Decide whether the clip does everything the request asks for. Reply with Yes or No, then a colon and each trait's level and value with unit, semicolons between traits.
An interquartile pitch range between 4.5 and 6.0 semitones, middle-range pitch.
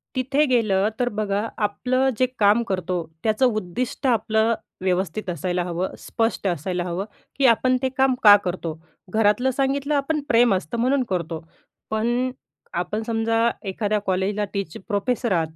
No: average, 4.9 semitones; high, 215 Hz